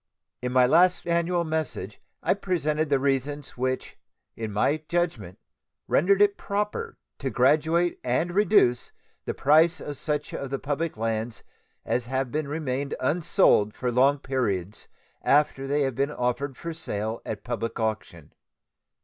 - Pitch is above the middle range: No, medium, 140 Hz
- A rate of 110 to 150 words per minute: Yes, average, 140 wpm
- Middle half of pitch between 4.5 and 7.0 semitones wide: Yes, average, 4.8 semitones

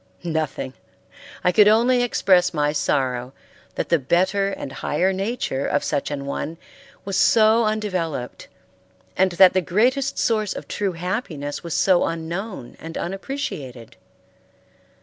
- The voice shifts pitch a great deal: Yes, wide, 5.9 semitones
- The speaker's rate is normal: No, slow, 130 wpm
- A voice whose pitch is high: No, medium, 180 Hz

